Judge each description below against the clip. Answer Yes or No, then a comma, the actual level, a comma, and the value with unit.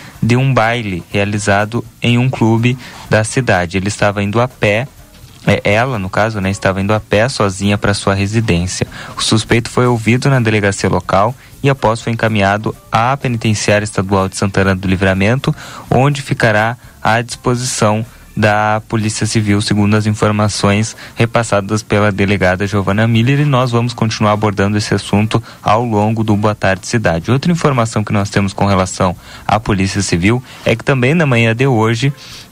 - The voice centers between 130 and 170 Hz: No, low, 110 Hz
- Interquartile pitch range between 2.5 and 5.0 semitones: Yes, average, 2.8 semitones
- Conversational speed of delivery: Yes, average, 165 wpm